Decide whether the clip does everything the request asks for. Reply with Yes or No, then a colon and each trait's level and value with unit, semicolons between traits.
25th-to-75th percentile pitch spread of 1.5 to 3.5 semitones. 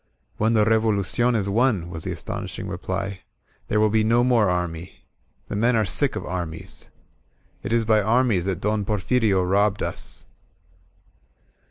Yes: average, 3.2 semitones